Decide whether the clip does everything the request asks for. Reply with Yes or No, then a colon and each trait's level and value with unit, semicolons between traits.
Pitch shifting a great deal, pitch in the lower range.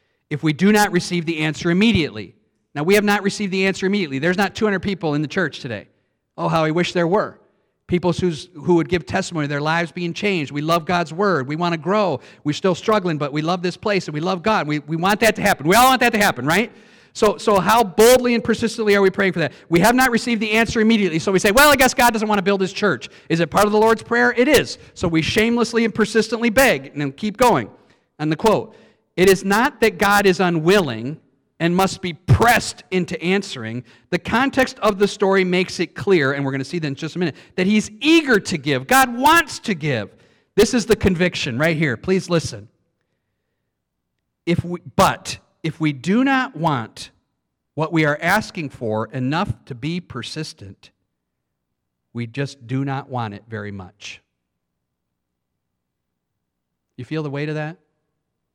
No: wide, 6.0 semitones; medium, 175 Hz